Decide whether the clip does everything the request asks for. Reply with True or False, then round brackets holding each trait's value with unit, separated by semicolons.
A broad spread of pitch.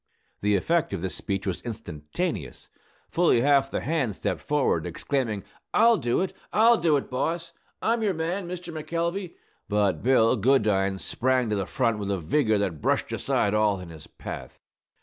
True (8.8 semitones)